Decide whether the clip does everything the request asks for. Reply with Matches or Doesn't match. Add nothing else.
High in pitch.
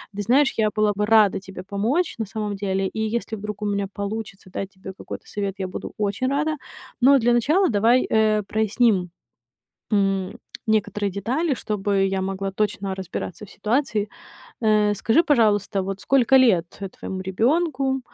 Matches